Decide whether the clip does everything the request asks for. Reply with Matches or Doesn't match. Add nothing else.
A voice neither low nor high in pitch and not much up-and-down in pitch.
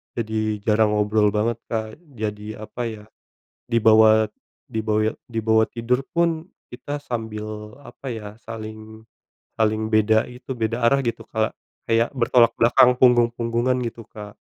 Doesn't match